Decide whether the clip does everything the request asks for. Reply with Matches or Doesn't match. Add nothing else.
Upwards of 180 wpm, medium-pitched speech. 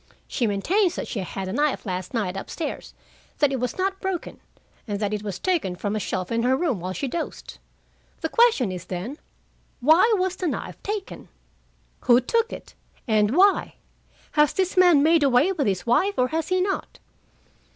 Doesn't match